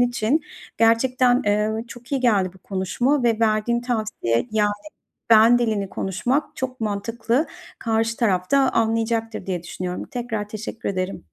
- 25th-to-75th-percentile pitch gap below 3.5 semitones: Yes, average, 2.7 semitones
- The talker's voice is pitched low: No, high, 225 Hz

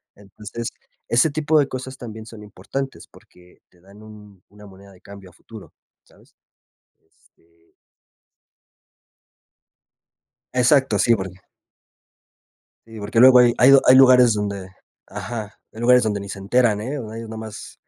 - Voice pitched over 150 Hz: No, low, 110 Hz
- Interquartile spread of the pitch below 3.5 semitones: No, average, 3.9 semitones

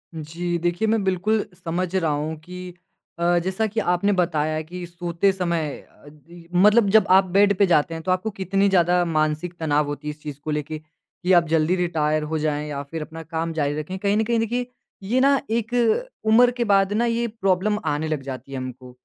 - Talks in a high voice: No, medium, 175 Hz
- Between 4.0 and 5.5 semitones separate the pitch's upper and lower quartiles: Yes, average, 4.3 semitones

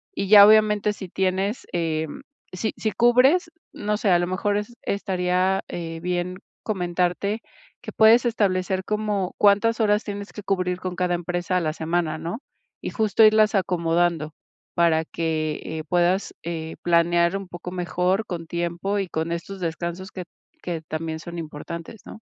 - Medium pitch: Yes, medium, 180 Hz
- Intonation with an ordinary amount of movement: Yes, average, 3.1 semitones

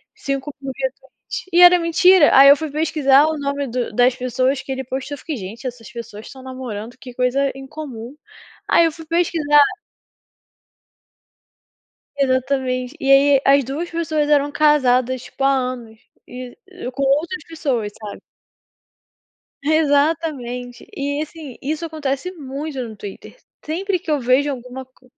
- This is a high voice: Yes, very high, 275 Hz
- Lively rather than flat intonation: No, average, 3.3 semitones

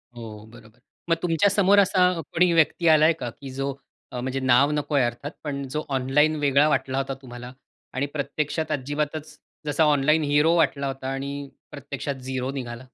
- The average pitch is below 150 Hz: Yes, medium, 140 Hz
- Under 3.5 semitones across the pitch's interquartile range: Yes, average, 2.8 semitones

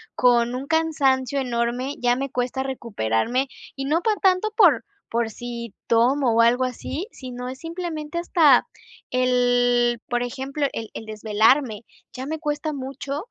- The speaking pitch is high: Yes, very high, 255 Hz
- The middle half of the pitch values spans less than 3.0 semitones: No, average, 3.3 semitones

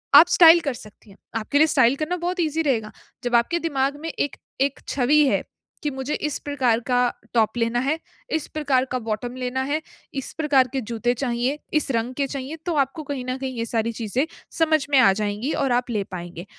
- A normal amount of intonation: Yes, average, 3.9 semitones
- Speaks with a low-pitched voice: No, very high, 265 Hz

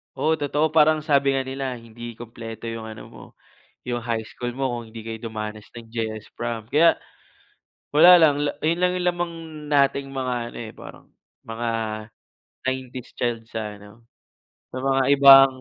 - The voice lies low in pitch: Yes, low, 125 Hz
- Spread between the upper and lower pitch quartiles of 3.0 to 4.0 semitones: Yes, average, 3.6 semitones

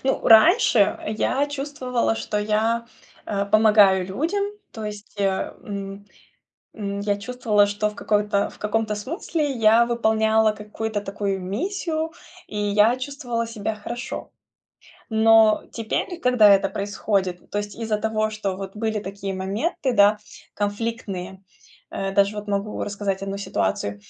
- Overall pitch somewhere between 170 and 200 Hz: No, high, 210 Hz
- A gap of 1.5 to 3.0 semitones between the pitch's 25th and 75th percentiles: Yes, narrow, 2.4 semitones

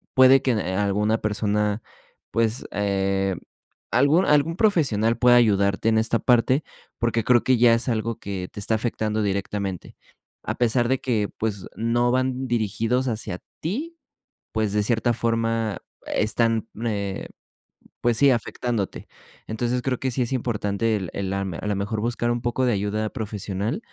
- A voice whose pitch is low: Yes, low, 115 Hz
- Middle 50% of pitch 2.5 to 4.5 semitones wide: Yes, average, 2.9 semitones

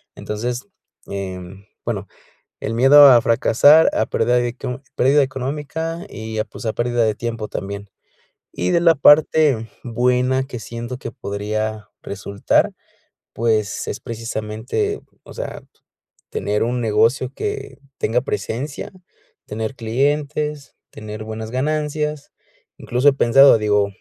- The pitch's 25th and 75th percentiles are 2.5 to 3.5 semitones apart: No, average, 4.2 semitones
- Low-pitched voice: Yes, low, 120 Hz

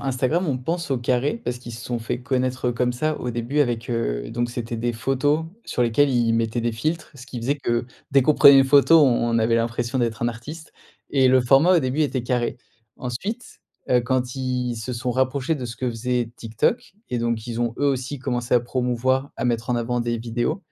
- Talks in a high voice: No, low, 125 Hz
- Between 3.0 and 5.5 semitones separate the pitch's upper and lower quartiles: No, narrow, 2.4 semitones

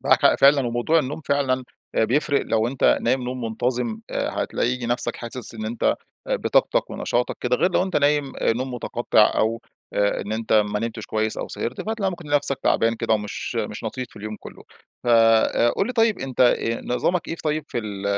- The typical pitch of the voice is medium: No, low, 125 Hz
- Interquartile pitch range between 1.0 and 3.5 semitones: No, average, 3.9 semitones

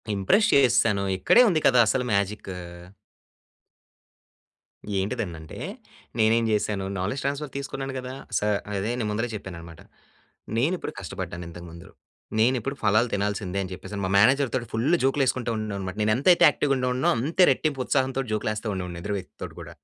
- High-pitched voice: No, low, 110 Hz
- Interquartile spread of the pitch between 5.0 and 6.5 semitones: Yes, average, 5.3 semitones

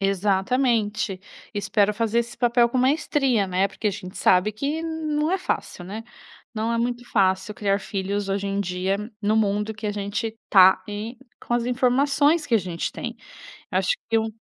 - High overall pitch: Yes, high, 215 Hz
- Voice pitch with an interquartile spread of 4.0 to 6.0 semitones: No, average, 3.6 semitones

